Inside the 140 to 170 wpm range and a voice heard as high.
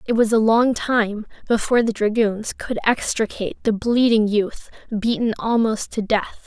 Yes: average, 160 wpm; high, 220 Hz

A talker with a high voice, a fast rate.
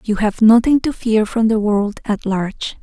Yes: high, 215 Hz; fast, 215 wpm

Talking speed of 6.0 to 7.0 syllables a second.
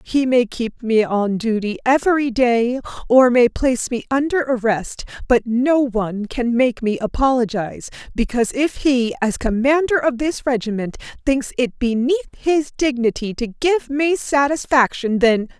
No: 4.5 syllables/s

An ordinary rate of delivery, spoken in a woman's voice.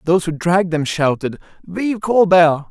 No: average, 155 wpm; male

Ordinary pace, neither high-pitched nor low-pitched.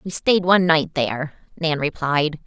Yes: average, 170 wpm; medium, 160 Hz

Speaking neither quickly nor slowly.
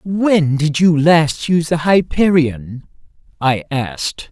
No: slow, 125 wpm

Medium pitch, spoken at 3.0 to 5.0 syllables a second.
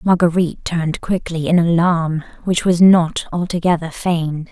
Yes: medium, 170 Hz; 4.8 syllables/s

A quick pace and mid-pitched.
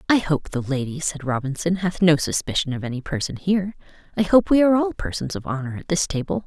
Yes: fast, 225 wpm; medium, 165 Hz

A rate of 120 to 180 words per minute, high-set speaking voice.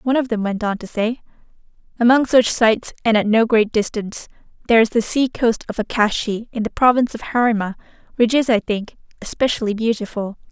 No: average, 190 wpm; high, 225 Hz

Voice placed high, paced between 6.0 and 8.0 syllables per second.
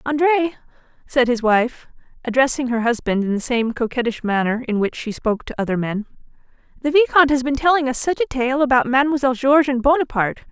Yes: very high, 255 Hz; 6.3 syllables/s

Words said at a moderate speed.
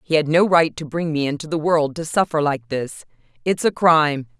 No: fast, 230 wpm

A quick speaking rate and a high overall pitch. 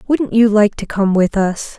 Yes: fast, 235 wpm; high, 210 Hz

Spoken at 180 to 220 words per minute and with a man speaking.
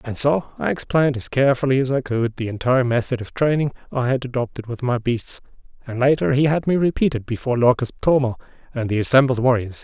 Yes: fast, 205 wpm; male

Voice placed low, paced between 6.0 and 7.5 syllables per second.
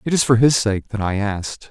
No: low, 110 Hz; 5.6 syllables/s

